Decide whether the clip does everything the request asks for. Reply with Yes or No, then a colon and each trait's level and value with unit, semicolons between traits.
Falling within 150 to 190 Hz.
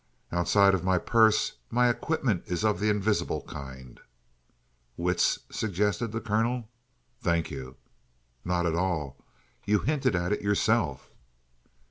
No: low, 100 Hz